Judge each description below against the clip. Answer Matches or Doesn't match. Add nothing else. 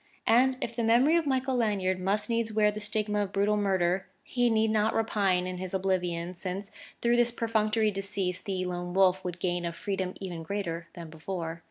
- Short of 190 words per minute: Doesn't match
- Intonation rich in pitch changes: Doesn't match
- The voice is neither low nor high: Doesn't match